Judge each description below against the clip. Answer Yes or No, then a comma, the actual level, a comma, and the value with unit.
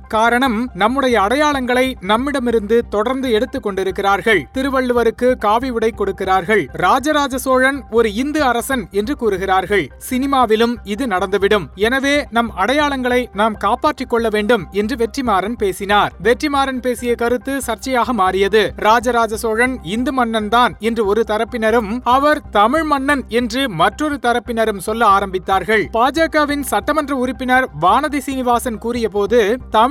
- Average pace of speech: Yes, average, 115 wpm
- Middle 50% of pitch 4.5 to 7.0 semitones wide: No, average, 3.4 semitones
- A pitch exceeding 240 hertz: No, high, 235 Hz